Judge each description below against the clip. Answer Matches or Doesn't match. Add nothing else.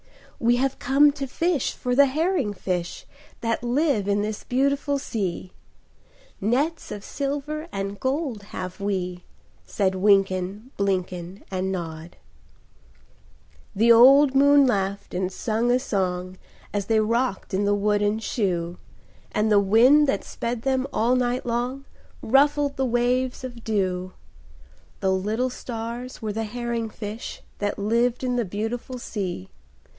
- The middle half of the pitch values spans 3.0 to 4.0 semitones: Doesn't match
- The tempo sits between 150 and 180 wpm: Doesn't match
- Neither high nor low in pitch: Doesn't match